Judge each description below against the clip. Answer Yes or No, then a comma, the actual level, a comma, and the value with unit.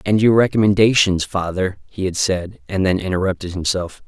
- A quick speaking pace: No, average, 160 wpm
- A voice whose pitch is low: Yes, very low, 95 Hz